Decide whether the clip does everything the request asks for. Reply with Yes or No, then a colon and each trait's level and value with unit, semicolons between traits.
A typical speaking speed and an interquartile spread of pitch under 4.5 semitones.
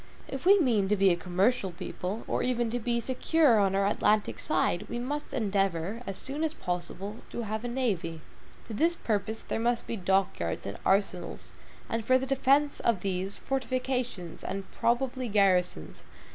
No: average, 175 wpm; average, 4.8 semitones